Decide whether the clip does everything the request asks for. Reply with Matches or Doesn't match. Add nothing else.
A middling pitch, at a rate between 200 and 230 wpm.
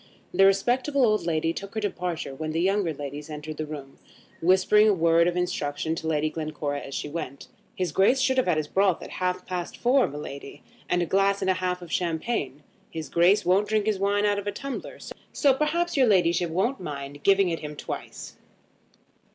Matches